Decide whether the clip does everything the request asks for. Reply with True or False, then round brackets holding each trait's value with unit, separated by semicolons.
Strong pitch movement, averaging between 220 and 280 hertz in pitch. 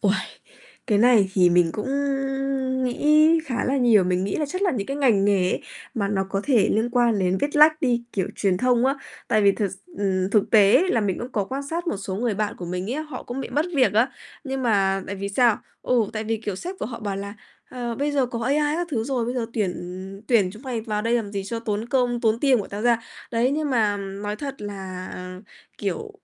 False (4.5 semitones; 225 Hz)